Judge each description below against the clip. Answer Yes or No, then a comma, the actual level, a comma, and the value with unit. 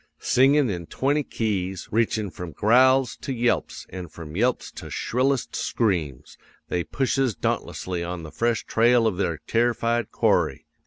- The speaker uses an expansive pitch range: Yes, wide, 5.7 semitones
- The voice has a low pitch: Yes, low, 115 Hz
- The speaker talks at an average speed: Yes, average, 145 wpm